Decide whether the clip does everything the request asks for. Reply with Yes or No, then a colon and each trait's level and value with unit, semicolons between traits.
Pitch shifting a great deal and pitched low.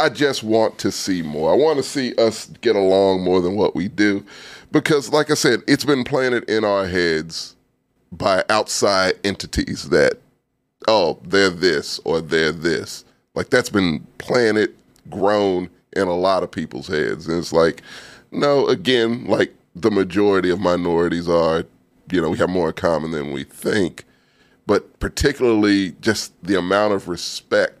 No: average, 4.7 semitones; low, 100 Hz